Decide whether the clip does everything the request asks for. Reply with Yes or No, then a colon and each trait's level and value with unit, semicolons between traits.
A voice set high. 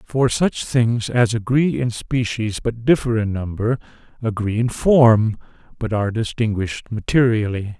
No: low, 115 Hz